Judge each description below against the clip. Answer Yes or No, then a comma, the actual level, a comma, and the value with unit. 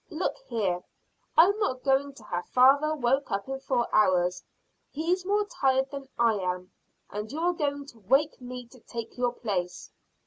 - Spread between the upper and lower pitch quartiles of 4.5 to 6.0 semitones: Yes, average, 5.1 semitones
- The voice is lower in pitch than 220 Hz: No, very high, 260 Hz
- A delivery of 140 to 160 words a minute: No, average, 175 wpm